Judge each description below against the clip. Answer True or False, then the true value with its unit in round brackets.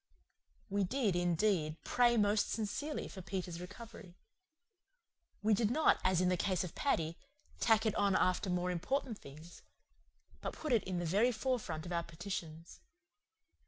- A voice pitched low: False (190 Hz)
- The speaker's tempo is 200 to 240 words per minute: False (155 wpm)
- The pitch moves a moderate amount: True (4.0 semitones)